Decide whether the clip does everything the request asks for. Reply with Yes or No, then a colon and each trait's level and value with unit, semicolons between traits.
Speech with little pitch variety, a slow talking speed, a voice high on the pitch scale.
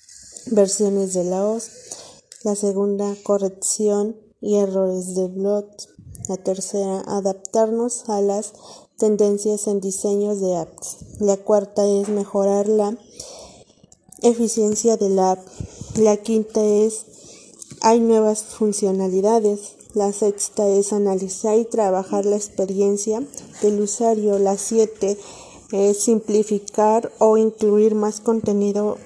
Yes: narrow, 1.5 semitones; slow, 115 wpm; high, 205 Hz